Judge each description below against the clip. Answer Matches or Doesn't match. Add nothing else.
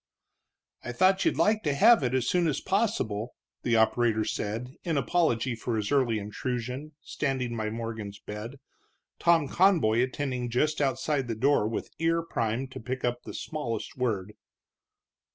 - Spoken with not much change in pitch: Doesn't match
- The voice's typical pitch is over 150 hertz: Doesn't match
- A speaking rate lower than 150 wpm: Doesn't match